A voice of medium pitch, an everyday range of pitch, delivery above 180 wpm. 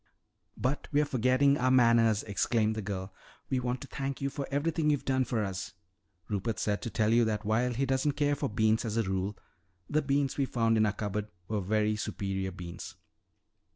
No: low, 115 Hz; average, 4.3 semitones; average, 195 wpm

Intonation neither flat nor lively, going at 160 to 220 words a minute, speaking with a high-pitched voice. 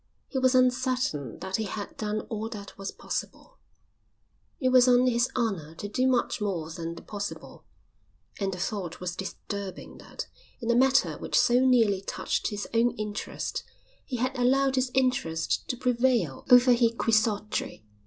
Yes: average, 4.3 semitones; average, 165 wpm; high, 225 Hz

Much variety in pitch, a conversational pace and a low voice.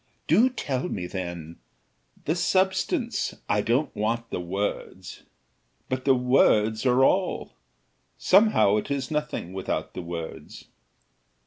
No: wide, 8.0 semitones; slow, 120 wpm; low, 125 Hz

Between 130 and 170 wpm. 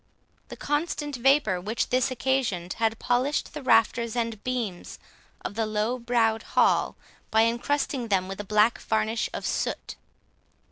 Yes: average, 145 wpm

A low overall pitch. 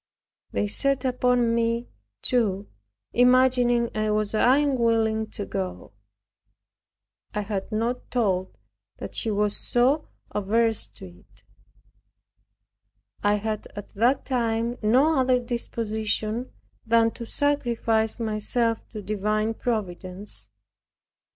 No: high, 225 Hz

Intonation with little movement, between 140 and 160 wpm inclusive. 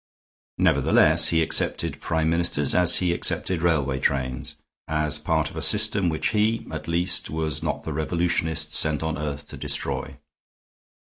Yes: narrow, 2.3 semitones; average, 150 wpm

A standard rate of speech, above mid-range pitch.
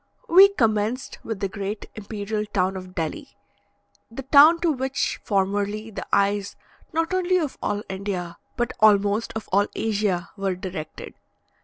Yes: average, 145 wpm; high, 210 Hz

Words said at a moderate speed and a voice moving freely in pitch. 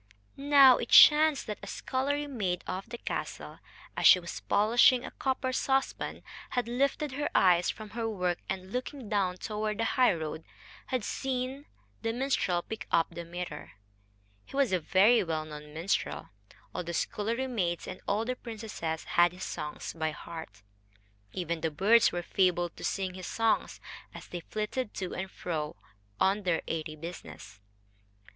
Yes: average, 165 wpm; wide, 6.1 semitones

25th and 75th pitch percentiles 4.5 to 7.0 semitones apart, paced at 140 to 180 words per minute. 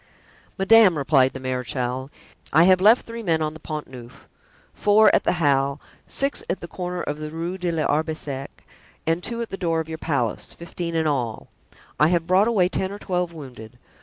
No: average, 4.8 semitones; average, 195 wpm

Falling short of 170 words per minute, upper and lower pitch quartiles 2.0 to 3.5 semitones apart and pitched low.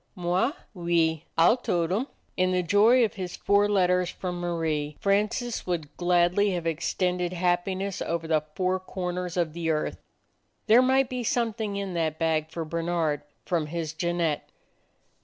No: average, 155 wpm; average, 3.1 semitones; medium, 175 Hz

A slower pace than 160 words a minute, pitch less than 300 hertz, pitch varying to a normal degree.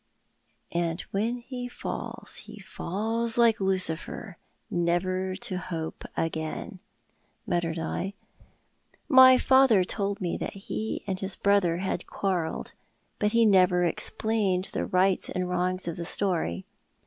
Yes: average, 140 wpm; medium, 185 Hz; average, 3.2 semitones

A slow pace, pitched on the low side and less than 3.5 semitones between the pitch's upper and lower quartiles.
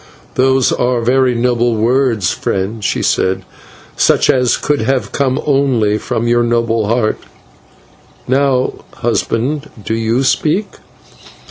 Yes: slow, 120 wpm; low, 120 Hz; narrow, 2.6 semitones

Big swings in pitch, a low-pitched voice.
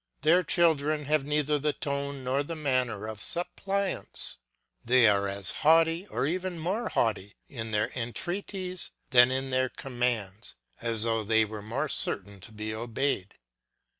Yes: wide, 6.0 semitones; low, 130 Hz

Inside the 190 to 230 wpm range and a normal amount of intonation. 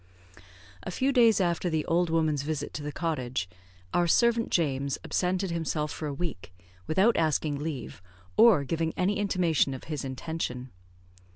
No: average, 155 wpm; average, 3.9 semitones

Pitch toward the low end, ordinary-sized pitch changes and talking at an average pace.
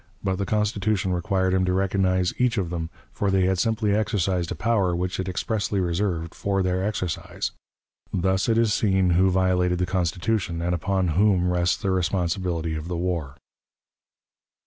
No: very low, 95 Hz; narrow, 2.0 semitones; average, 170 wpm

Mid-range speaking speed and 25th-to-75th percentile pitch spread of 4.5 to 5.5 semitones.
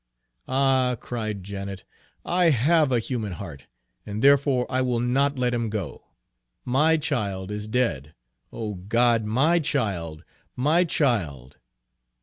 No: slow, 130 wpm; average, 5.2 semitones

